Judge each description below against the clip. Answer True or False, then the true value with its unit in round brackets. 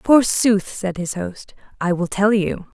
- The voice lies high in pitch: True (195 Hz)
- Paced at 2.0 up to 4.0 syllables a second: True (3.7 syllables/s)